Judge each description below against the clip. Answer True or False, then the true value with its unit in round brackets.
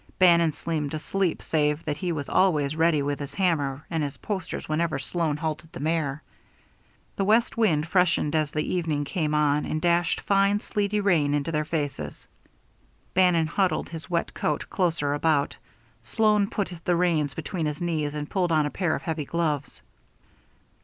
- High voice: False (160 Hz)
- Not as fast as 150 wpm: False (175 wpm)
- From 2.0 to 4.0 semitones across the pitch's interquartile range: True (3.1 semitones)